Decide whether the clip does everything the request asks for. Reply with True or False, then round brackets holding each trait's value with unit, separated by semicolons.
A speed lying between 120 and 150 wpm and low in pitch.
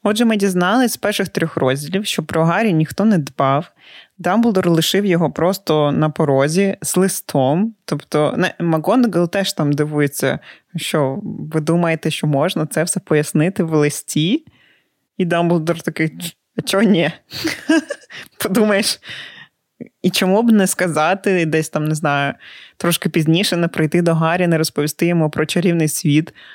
False (145 wpm; 170 Hz)